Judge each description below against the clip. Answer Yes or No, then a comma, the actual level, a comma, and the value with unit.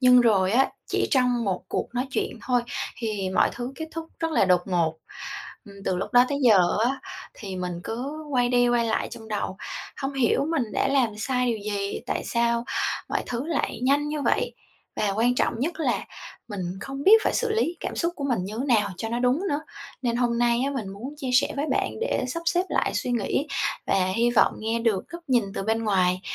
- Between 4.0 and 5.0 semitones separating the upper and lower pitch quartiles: Yes, average, 4.3 semitones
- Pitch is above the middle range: Yes, high, 240 Hz